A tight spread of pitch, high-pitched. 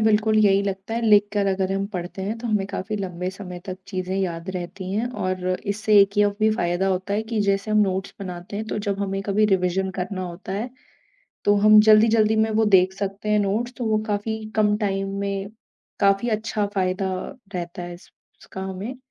Yes: narrow, 2.1 semitones; high, 195 Hz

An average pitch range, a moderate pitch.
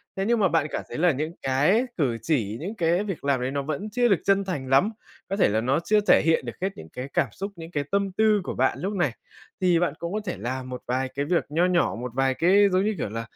No: wide, 6.7 semitones; medium, 165 Hz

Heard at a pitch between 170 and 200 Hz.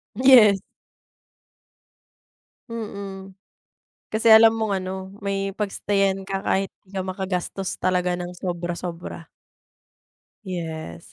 Yes: high, 190 Hz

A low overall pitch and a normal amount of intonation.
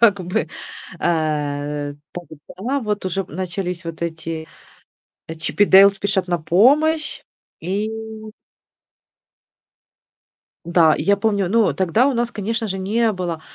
No: medium, 185 Hz; average, 4.2 semitones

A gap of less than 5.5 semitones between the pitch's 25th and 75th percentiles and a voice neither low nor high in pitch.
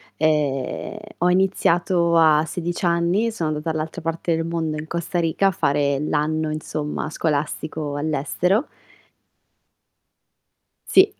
Yes: narrow, 2.4 semitones; medium, 160 Hz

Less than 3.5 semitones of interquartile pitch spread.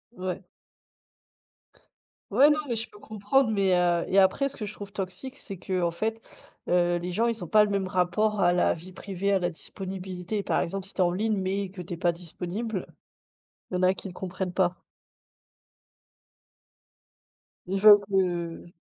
Yes: average, 2.7 semitones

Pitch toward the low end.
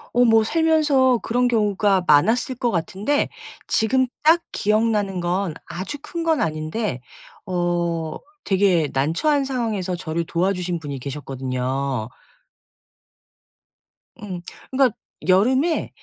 No: high, 195 Hz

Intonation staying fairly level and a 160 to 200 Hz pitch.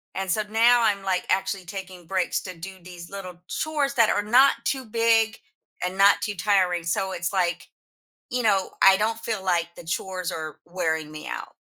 No: average, 3.6 semitones; high, 190 Hz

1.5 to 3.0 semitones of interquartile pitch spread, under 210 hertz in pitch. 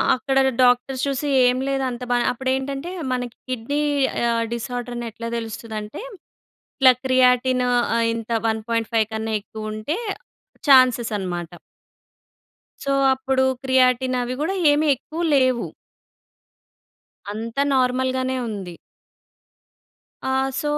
No: narrow, 2.4 semitones; very high, 250 Hz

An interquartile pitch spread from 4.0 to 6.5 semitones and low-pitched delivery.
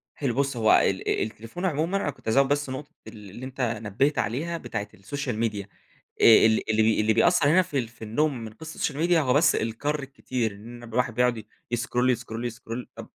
Yes: average, 4.3 semitones; low, 125 Hz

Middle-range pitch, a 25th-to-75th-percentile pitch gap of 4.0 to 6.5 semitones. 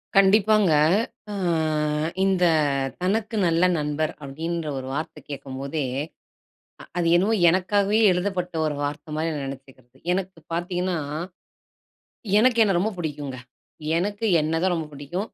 Yes: medium, 175 Hz; average, 4.6 semitones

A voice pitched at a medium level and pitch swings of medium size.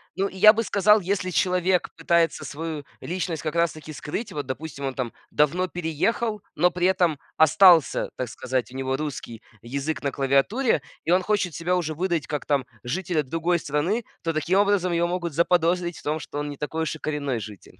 Yes: medium, 165 Hz; average, 3.8 semitones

